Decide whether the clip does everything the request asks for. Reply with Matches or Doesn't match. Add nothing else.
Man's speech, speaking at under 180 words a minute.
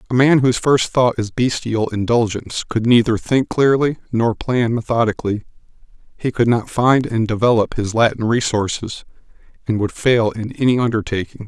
Matches